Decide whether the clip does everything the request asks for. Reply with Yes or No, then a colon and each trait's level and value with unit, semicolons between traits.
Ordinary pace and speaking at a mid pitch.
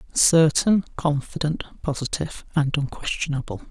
No: slow, 80 wpm; medium, 150 Hz